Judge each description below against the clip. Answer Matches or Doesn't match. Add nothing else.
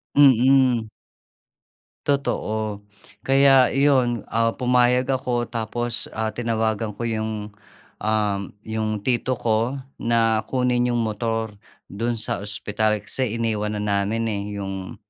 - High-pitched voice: Doesn't match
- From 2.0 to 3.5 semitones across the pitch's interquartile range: Matches